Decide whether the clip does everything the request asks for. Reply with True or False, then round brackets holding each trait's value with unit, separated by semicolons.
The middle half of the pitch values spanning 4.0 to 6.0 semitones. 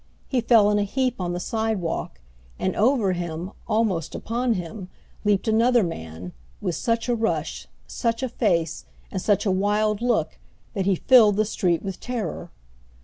True (4.3 semitones)